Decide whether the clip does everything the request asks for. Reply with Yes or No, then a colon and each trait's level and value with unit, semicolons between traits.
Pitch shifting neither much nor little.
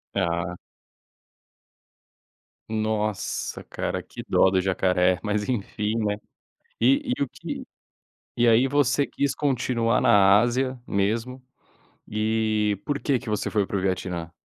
Yes: average, 4.2 semitones